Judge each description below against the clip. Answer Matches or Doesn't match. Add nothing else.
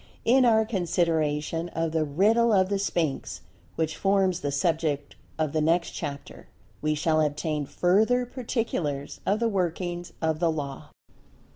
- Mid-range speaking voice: Matches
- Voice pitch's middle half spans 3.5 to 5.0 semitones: Matches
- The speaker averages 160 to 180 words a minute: Doesn't match